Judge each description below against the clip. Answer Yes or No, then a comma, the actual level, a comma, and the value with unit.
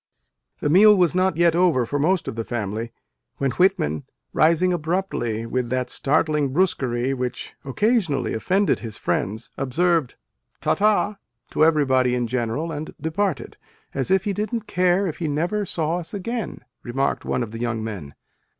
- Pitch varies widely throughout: Yes, wide, 6.9 semitones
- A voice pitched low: No, medium, 155 Hz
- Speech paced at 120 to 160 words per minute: No, average, 170 wpm